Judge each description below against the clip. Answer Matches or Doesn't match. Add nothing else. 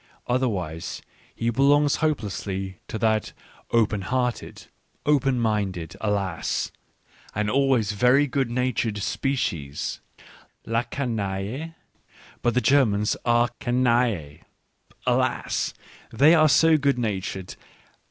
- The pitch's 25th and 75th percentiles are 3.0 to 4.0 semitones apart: Doesn't match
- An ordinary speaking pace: Doesn't match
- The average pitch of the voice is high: Doesn't match